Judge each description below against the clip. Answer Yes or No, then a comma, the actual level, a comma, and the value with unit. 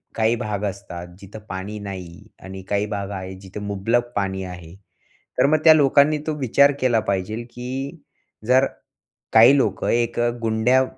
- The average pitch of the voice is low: Yes, low, 105 Hz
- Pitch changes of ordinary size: Yes, average, 4.8 semitones